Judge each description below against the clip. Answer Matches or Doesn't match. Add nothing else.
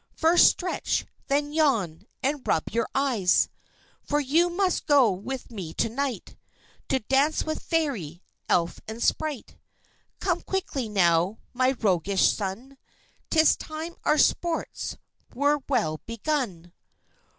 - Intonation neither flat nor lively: Doesn't match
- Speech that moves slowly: Matches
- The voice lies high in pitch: Matches